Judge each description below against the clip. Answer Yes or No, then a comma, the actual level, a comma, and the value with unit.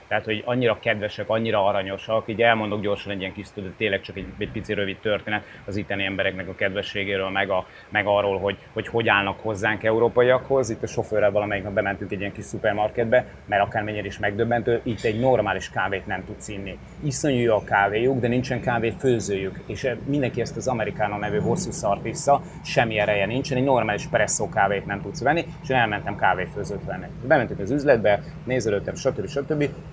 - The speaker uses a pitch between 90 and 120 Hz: Yes, low, 105 Hz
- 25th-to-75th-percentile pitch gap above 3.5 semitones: No, average, 2.9 semitones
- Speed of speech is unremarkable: No, fast, 190 wpm